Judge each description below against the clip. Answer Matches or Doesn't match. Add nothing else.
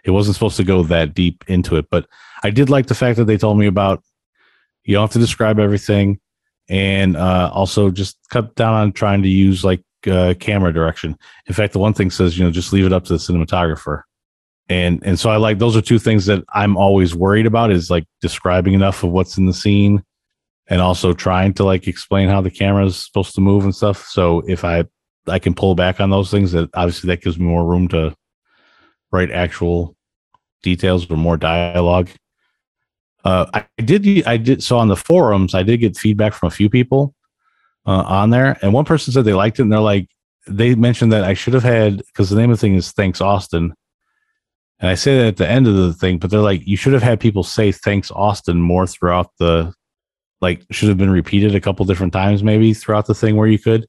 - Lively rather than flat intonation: Doesn't match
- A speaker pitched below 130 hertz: Matches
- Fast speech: Matches